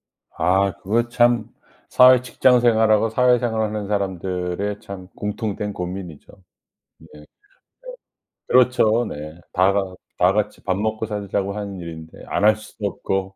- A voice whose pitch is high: No, low, 105 Hz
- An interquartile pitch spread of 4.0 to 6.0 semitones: No, average, 2.9 semitones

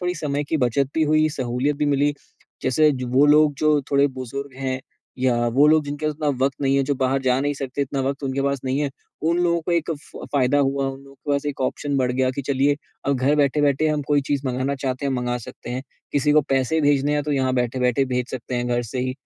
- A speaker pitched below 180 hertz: Yes, medium, 140 Hz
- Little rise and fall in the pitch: Yes, narrow, 2.1 semitones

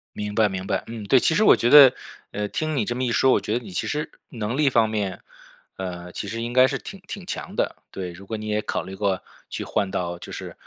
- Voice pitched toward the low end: Yes, low, 110 Hz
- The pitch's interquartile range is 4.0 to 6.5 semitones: Yes, average, 4.7 semitones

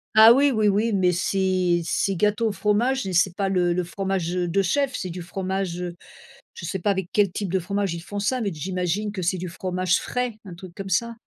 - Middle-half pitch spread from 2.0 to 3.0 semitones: Yes, narrow, 2.6 semitones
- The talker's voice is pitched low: No, high, 190 Hz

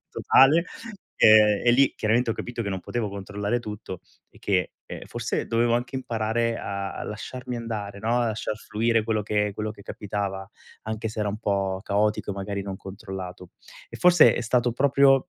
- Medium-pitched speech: No, low, 110 Hz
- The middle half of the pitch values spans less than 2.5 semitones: No, average, 2.8 semitones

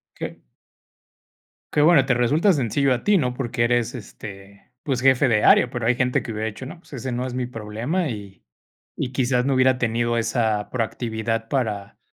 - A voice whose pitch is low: Yes, low, 120 Hz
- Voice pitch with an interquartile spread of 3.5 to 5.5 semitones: No, average, 2.7 semitones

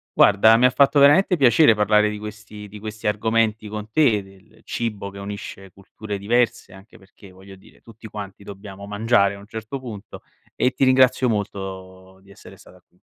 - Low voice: Yes, low, 105 Hz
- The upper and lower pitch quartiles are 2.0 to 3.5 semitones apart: Yes, narrow, 2.4 semitones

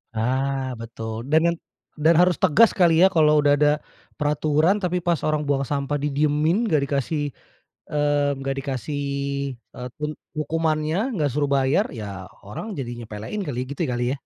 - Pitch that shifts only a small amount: No, average, 3.0 semitones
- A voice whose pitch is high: No, medium, 145 Hz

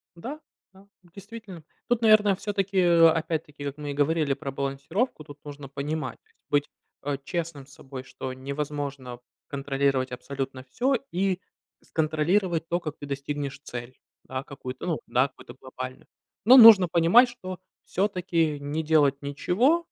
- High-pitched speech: No, medium, 150 Hz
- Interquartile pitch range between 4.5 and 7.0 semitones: Yes, average, 4.9 semitones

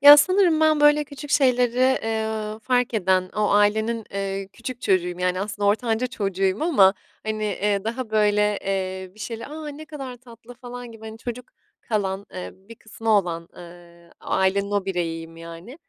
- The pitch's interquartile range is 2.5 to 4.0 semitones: No, average, 4.4 semitones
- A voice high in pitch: Yes, high, 215 Hz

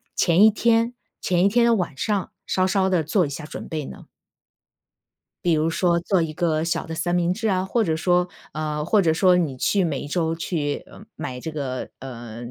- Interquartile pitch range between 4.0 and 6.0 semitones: No, average, 3.5 semitones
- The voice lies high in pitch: No, medium, 170 Hz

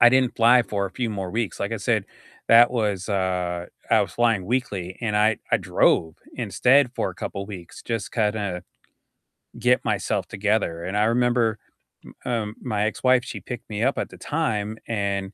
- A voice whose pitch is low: Yes, low, 110 Hz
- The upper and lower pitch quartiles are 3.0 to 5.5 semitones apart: Yes, average, 3.4 semitones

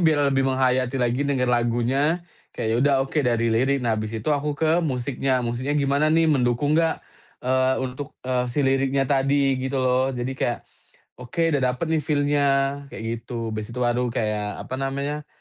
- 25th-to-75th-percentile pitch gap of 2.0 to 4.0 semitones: Yes, average, 2.7 semitones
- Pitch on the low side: Yes, low, 130 Hz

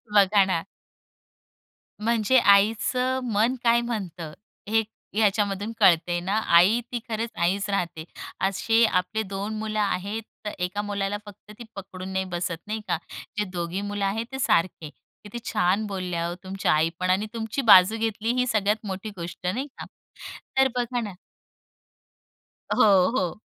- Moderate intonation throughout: Yes, average, 3.3 semitones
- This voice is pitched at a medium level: No, high, 200 Hz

